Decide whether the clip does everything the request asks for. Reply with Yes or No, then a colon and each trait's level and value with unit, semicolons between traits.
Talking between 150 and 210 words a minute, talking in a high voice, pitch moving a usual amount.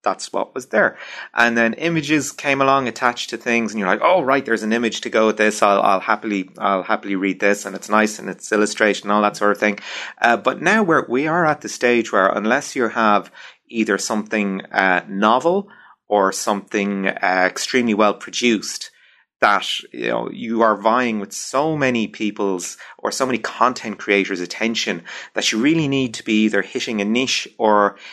No: average, 200 wpm; low, 110 Hz; average, 3.1 semitones